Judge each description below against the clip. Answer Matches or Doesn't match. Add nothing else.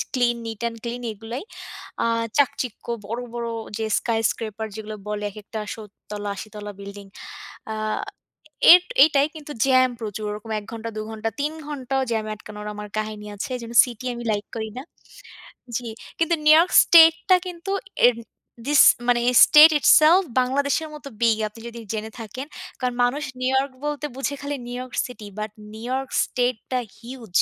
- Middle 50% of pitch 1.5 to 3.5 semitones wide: Doesn't match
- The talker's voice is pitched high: Matches